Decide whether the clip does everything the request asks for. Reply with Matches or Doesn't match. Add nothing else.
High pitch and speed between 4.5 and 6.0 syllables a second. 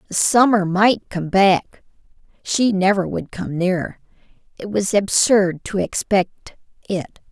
Doesn't match